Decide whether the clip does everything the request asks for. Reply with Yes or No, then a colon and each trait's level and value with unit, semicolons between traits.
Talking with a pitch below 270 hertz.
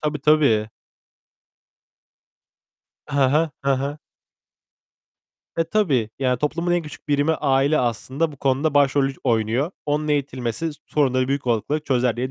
Yes: medium, 140 Hz